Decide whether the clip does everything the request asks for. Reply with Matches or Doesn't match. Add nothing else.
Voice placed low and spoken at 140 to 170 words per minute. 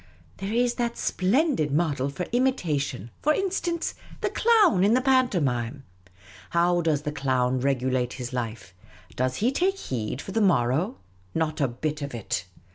Doesn't match